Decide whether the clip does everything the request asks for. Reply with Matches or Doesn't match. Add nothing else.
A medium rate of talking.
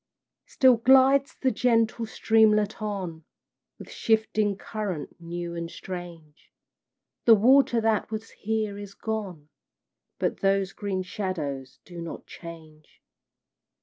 Doesn't match